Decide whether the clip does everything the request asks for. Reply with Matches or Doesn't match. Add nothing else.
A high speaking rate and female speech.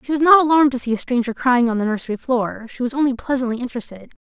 Matches